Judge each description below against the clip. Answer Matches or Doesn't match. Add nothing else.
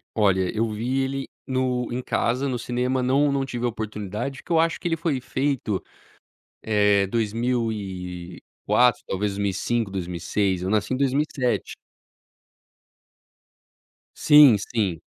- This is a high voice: Doesn't match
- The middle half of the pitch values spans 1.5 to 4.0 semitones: Doesn't match